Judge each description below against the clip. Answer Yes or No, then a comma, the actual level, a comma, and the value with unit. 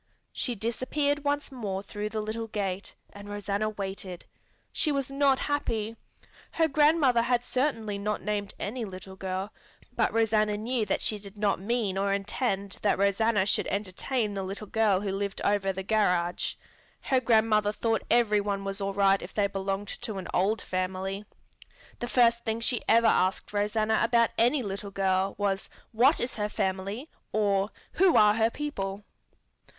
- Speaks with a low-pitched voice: No, high, 210 Hz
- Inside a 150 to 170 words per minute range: Yes, average, 165 wpm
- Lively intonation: No, average, 2.9 semitones